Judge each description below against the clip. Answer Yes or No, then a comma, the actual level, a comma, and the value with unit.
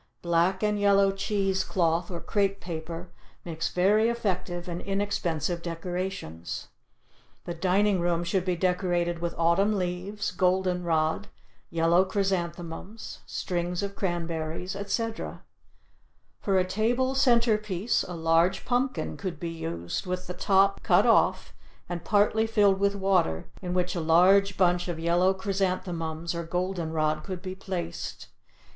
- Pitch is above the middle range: No, medium, 180 Hz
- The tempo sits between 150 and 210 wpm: No, average, 140 wpm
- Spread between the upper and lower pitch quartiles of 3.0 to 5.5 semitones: No, narrow, 2.6 semitones